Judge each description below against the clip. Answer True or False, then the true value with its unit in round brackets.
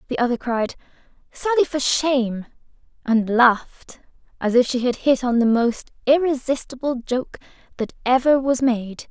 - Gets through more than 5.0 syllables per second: False (4.6 syllables/s)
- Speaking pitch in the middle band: False (250 Hz)